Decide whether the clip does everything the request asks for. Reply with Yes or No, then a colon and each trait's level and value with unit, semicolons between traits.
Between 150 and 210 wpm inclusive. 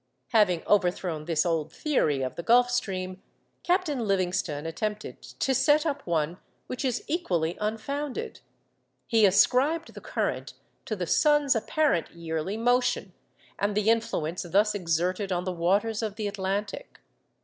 No: average, 140 wpm